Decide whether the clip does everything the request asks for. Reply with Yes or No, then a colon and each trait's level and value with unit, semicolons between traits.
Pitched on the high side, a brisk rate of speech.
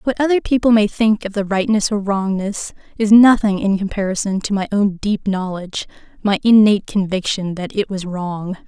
No: high, 200 Hz; average, 180 wpm